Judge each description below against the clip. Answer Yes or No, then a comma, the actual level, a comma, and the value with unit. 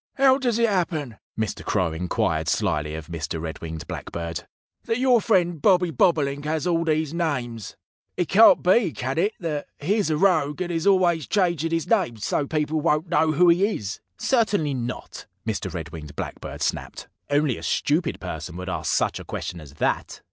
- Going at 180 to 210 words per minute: Yes, average, 185 wpm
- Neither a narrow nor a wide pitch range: No, wide, 8.6 semitones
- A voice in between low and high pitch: Yes, medium, 155 Hz